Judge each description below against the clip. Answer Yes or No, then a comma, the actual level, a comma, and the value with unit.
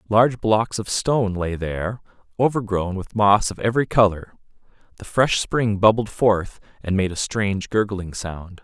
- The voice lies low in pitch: Yes, low, 105 Hz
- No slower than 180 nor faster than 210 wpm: No, average, 160 wpm